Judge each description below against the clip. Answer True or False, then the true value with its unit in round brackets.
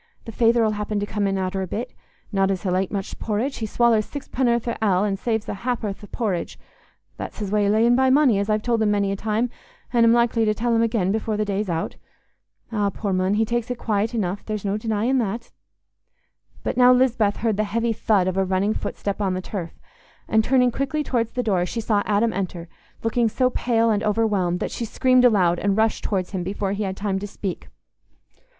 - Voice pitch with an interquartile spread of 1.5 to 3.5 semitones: True (2.9 semitones)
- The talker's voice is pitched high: True (215 Hz)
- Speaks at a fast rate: True (220 wpm)